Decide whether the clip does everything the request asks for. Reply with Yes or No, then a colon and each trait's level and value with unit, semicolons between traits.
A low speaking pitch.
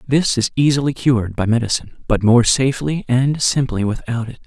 Yes: low, 125 Hz